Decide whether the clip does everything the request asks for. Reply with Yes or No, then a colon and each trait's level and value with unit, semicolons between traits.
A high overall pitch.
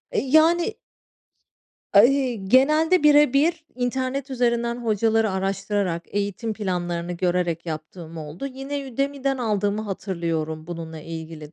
Yes: high, 215 Hz